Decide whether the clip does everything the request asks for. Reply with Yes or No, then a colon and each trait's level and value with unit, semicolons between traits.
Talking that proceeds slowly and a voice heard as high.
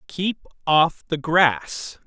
No: slow, 115 wpm; medium, 160 Hz